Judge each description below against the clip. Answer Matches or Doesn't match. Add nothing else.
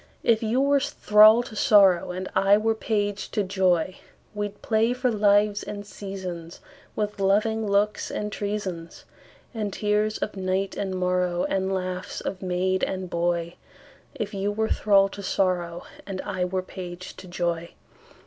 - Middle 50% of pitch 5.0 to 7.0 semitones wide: Doesn't match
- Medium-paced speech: Doesn't match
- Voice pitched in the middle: Doesn't match